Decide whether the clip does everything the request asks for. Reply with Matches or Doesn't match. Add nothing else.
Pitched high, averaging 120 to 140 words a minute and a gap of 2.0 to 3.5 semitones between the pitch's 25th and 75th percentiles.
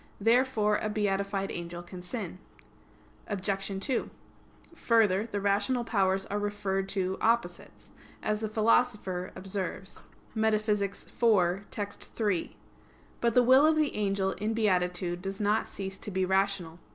Matches